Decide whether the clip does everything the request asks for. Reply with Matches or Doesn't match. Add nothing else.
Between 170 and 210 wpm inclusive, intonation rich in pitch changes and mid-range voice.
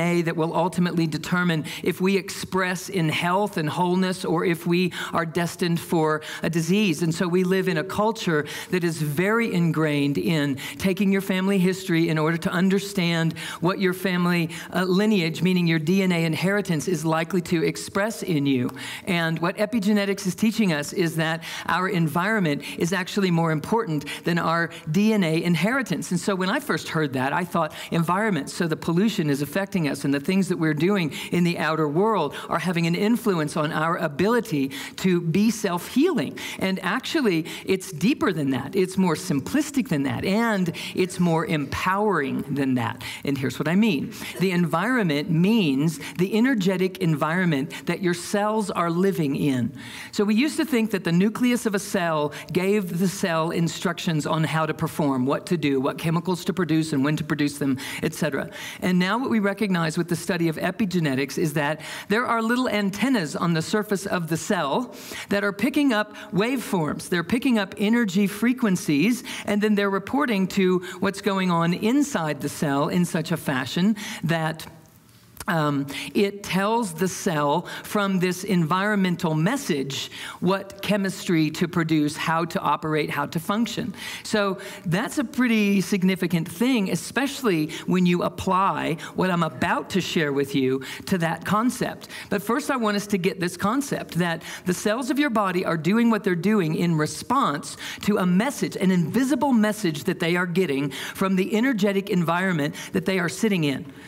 Doesn't match